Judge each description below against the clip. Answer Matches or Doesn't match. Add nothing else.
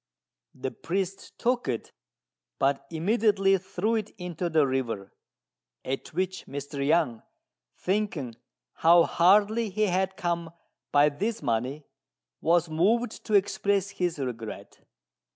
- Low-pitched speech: Doesn't match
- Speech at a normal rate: Doesn't match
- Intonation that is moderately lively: Doesn't match